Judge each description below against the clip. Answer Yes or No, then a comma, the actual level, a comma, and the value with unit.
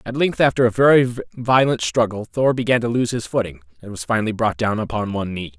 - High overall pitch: No, low, 115 Hz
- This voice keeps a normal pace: No, fast, 225 wpm